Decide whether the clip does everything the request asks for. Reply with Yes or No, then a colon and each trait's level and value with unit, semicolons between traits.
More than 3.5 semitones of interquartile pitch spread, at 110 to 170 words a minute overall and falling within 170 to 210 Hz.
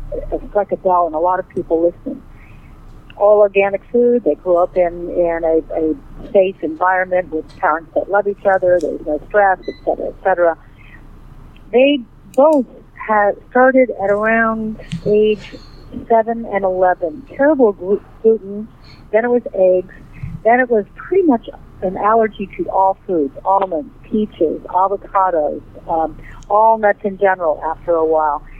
Yes: average, 4.6 semitones; average, 150 wpm; high, 190 Hz